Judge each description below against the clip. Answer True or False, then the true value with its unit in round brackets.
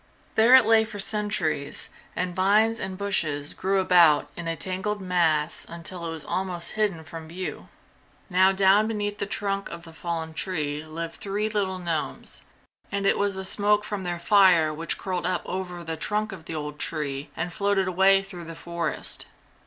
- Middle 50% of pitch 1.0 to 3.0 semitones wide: False (3.4 semitones)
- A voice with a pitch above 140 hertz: True (185 Hz)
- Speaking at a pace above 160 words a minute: True (180 wpm)